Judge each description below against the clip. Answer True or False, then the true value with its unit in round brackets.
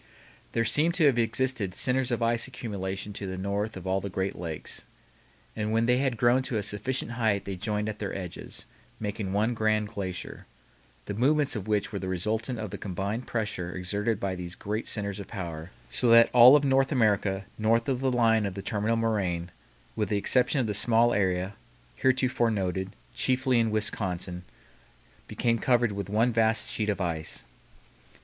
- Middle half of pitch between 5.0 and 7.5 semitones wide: False (3.4 semitones)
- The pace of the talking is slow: False (185 wpm)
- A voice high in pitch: False (110 Hz)